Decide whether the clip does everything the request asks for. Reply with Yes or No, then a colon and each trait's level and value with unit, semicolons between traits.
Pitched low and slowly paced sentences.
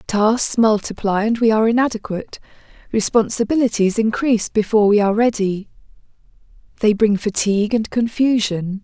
No: high, 220 Hz; slow, 115 wpm